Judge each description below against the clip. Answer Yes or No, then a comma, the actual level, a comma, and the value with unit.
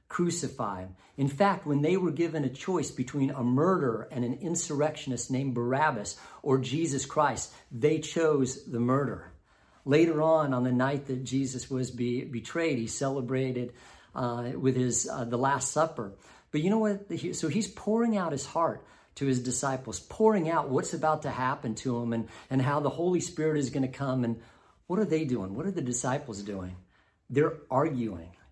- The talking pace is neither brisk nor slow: Yes, average, 180 wpm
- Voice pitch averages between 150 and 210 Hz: No, low, 135 Hz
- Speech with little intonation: No, average, 4.3 semitones